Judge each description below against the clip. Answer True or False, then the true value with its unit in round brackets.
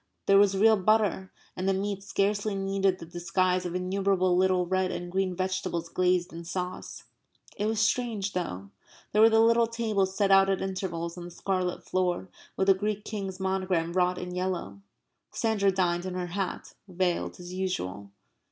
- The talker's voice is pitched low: False (185 Hz)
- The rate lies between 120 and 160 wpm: False (175 wpm)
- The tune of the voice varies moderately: False (1.7 semitones)